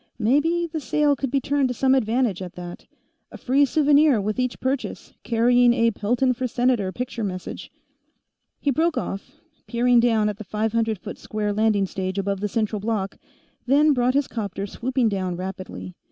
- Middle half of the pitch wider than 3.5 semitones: Yes, average, 4.3 semitones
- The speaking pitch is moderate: No, high, 235 Hz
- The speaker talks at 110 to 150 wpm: No, average, 180 wpm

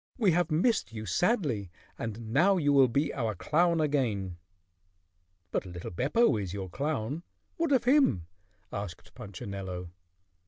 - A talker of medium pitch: No, low, 130 Hz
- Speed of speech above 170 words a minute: No, slow, 135 wpm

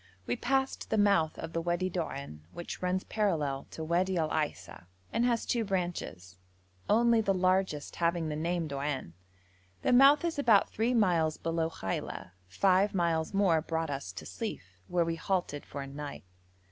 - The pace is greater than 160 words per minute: Yes, average, 170 wpm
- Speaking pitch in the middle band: Yes, medium, 170 Hz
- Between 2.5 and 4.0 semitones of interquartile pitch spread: No, average, 4.8 semitones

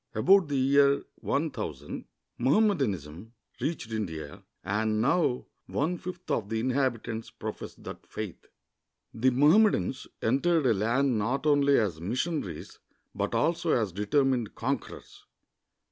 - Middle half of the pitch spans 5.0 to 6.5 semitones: Yes, wide, 5.4 semitones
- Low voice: Yes, low, 130 Hz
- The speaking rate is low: Yes, slow, 120 wpm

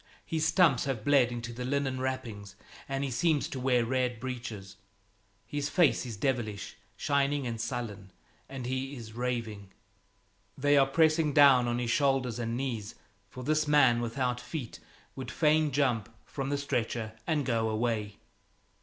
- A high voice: No, low, 125 Hz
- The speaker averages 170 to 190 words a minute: No, average, 155 wpm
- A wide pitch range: No, average, 3.3 semitones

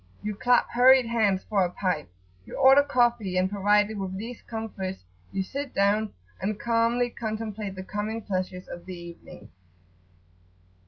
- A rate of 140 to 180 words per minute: Yes, average, 150 wpm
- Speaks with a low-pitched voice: No, high, 210 Hz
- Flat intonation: No, average, 3.6 semitones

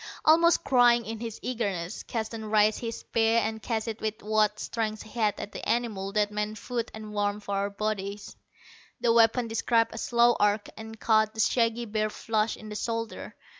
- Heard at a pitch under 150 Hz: No, high, 220 Hz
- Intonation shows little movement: Yes, narrow, 1.6 semitones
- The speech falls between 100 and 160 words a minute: No, average, 190 wpm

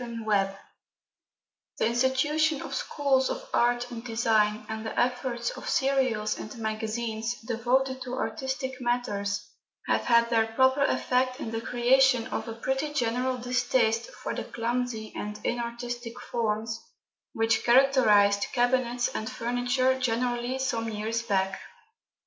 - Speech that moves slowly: Yes, slow, 130 wpm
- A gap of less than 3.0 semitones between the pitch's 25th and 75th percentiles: Yes, narrow, 2.4 semitones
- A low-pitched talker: No, high, 240 Hz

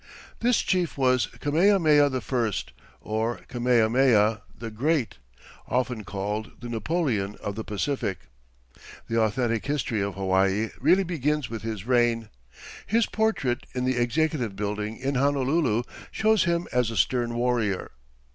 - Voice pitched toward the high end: No, low, 120 Hz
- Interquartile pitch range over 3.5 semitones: Yes, average, 4.9 semitones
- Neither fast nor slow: No, slow, 130 wpm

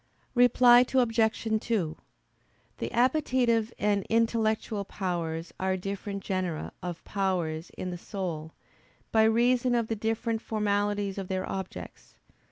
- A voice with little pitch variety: No, average, 3.6 semitones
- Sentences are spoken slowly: Yes, slow, 120 wpm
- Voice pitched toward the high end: Yes, high, 205 Hz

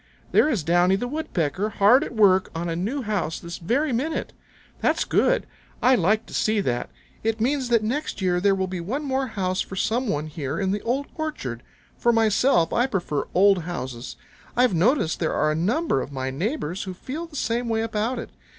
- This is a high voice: Yes, high, 205 Hz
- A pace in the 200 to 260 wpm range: Yes, fast, 205 wpm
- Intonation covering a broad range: Yes, wide, 6.3 semitones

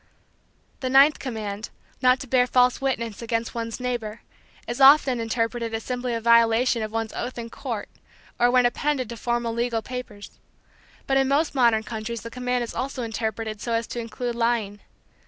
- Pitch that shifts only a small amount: Yes, narrow, 1.8 semitones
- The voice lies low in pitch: No, high, 235 Hz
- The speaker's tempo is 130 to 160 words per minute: No, average, 175 wpm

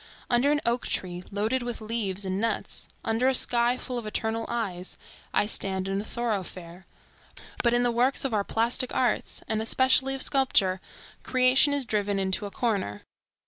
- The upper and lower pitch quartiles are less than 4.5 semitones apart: Yes, average, 4.1 semitones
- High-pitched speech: Yes, high, 225 Hz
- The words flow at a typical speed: Yes, average, 175 wpm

